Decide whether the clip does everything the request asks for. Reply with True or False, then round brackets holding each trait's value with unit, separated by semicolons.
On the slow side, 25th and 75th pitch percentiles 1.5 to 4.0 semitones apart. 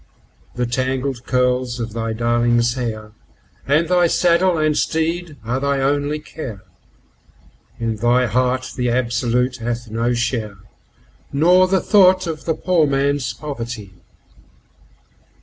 False (120 wpm; 4.5 semitones)